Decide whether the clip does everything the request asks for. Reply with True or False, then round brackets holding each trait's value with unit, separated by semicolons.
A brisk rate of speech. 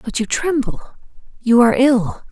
False (130 wpm)